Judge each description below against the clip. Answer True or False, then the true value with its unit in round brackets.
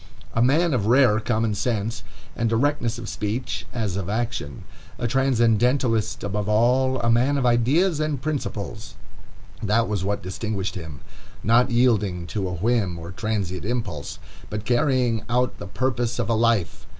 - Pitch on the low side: True (115 Hz)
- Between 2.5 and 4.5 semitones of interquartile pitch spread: True (3.3 semitones)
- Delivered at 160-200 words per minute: False (150 wpm)